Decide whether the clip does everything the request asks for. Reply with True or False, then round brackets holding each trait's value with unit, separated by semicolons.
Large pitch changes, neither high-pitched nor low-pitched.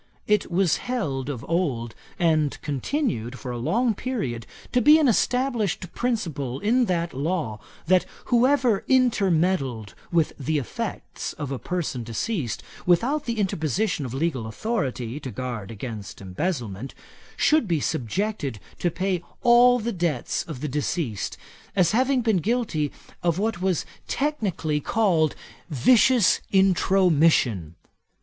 True (8.8 semitones; 170 Hz)